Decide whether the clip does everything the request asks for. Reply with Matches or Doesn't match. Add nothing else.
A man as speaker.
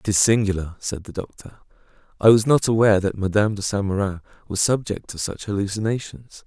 Matches